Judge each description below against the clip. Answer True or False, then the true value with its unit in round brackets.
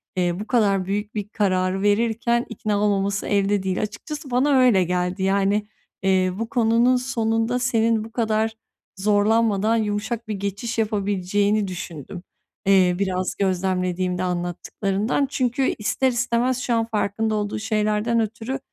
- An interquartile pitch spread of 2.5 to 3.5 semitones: True (3.0 semitones)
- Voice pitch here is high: True (210 Hz)